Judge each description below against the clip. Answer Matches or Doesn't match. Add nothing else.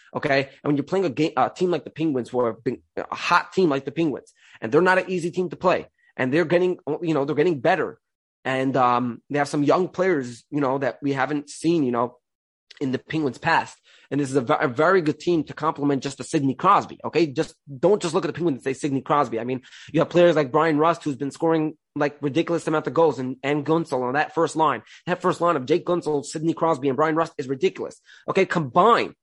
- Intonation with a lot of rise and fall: Doesn't match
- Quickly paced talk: Matches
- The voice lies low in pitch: Doesn't match